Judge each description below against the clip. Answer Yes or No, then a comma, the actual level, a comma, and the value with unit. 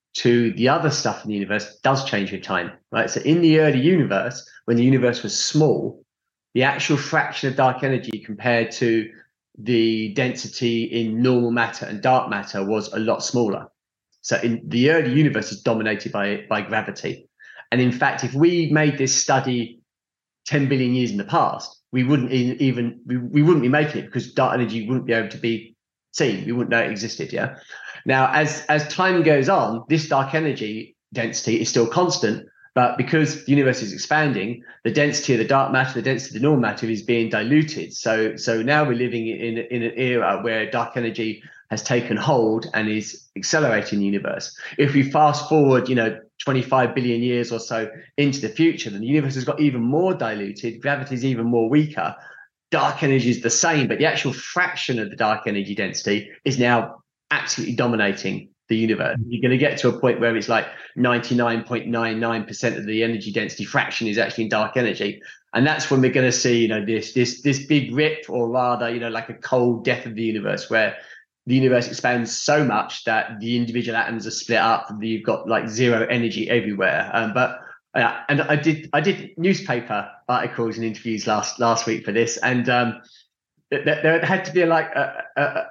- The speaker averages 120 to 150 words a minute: No, average, 200 wpm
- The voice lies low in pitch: Yes, low, 120 Hz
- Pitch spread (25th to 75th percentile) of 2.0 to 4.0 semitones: Yes, average, 3.3 semitones